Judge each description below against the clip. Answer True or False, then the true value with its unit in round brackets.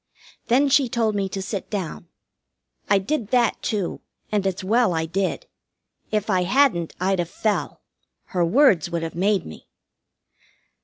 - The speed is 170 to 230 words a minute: False (155 wpm)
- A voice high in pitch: True (200 Hz)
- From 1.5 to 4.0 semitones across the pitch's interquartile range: False (4.5 semitones)